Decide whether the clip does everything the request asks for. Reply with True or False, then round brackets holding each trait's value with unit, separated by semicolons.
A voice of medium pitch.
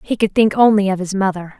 False (200 Hz)